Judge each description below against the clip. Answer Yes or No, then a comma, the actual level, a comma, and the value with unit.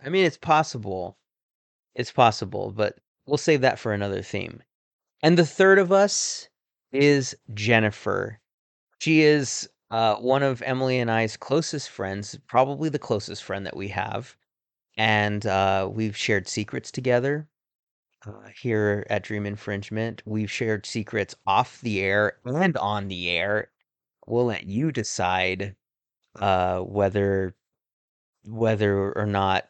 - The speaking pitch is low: Yes, low, 110 Hz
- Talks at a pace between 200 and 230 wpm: No, slow, 135 wpm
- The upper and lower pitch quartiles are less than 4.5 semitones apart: No, average, 4.9 semitones